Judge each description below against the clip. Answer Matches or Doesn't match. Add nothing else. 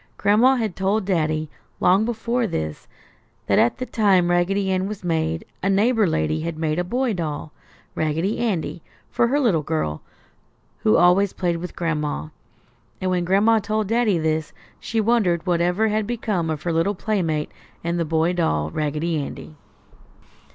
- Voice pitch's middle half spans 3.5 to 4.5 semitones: Doesn't match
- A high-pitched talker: Doesn't match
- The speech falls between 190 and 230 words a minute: Doesn't match